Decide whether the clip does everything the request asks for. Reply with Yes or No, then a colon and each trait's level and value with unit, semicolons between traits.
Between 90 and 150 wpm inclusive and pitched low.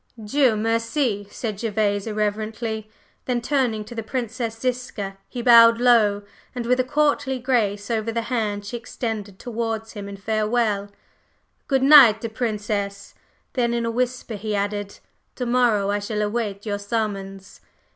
No: average, 145 wpm; high, 225 Hz